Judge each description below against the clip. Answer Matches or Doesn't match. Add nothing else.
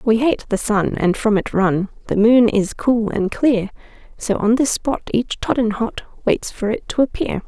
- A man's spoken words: Doesn't match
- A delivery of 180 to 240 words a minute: Matches